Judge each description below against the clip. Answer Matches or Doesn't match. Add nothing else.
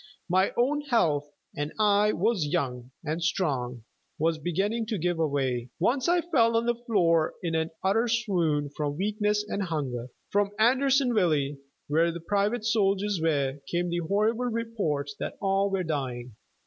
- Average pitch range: Doesn't match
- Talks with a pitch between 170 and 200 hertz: Matches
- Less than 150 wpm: Doesn't match